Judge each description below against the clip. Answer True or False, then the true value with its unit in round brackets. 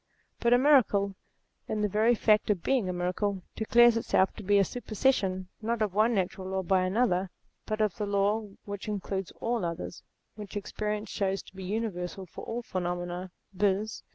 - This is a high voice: True (205 Hz)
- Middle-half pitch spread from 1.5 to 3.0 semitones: True (2.6 semitones)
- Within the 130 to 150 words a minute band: False (180 wpm)